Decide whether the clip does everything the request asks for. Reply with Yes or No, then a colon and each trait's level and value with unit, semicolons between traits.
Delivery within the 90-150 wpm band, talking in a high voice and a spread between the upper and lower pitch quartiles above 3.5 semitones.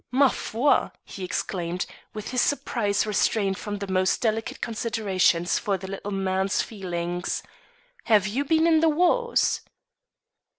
Yes: slow, 135 wpm; high, 205 Hz; average, 4.5 semitones